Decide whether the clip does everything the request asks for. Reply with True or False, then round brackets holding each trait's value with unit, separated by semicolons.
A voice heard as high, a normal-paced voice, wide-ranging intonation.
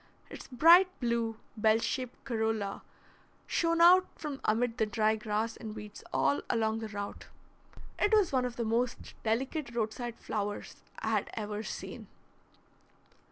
False (225 Hz; 145 wpm; 2.8 semitones)